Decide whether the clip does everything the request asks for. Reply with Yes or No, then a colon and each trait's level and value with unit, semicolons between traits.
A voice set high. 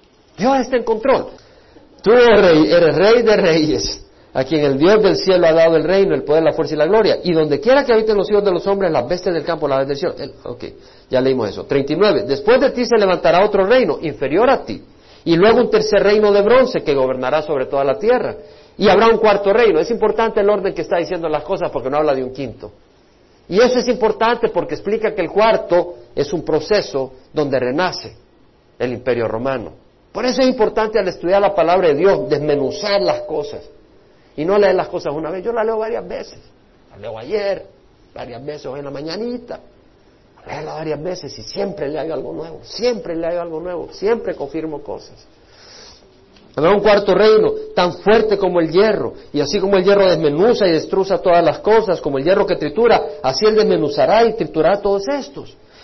Yes: high, 195 Hz